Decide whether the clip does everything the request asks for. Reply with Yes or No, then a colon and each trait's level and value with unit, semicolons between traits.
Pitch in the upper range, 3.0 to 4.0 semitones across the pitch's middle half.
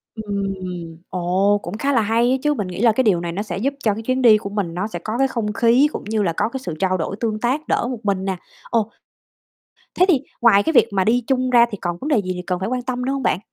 No: high, 220 Hz; average, 4.4 semitones